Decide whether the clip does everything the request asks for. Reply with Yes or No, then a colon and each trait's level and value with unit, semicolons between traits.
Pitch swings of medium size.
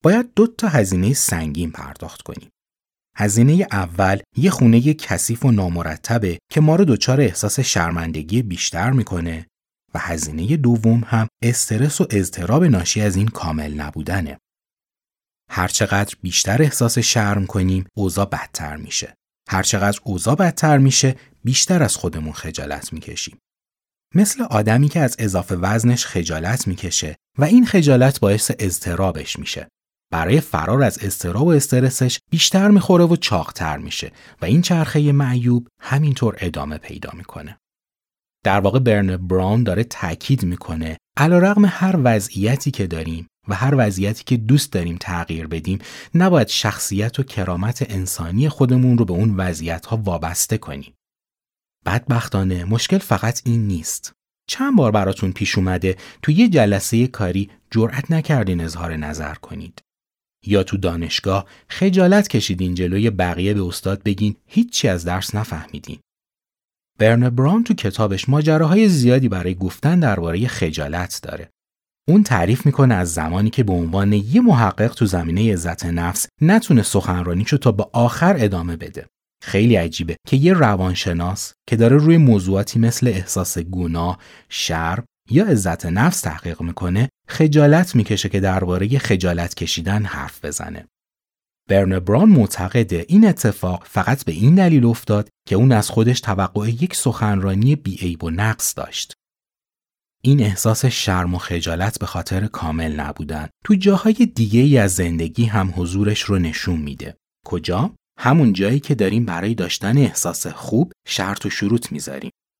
No: wide, 6.4 semitones